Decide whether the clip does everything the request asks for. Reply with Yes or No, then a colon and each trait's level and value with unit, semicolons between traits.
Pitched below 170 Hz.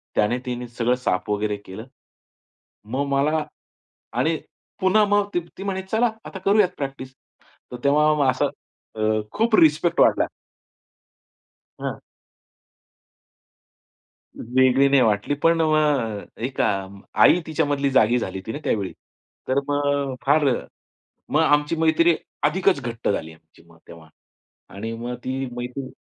Yes: medium, 140 Hz